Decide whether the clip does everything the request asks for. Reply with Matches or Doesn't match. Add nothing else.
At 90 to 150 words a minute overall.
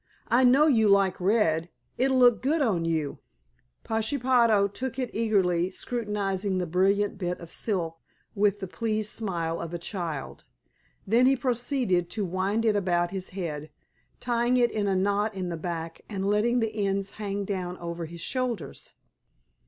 Doesn't match